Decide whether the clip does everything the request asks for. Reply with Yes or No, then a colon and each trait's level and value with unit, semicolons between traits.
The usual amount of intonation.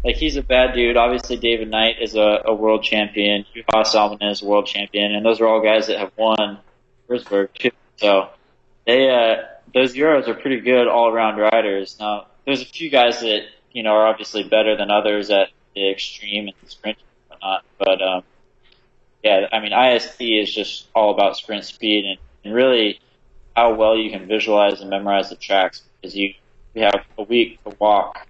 No: narrow, 2.2 semitones